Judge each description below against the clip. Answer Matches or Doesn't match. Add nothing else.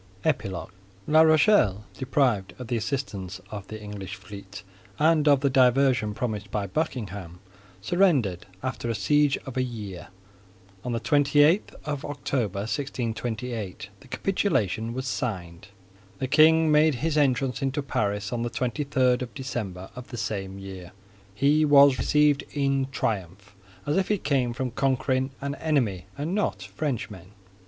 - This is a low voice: Matches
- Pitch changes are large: Matches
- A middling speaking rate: Matches